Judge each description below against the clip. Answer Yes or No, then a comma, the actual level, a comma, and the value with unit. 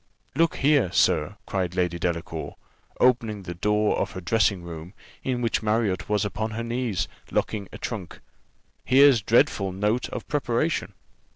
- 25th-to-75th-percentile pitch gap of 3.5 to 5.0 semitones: Yes, average, 4.3 semitones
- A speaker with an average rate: Yes, average, 150 wpm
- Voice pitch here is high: No, low, 105 Hz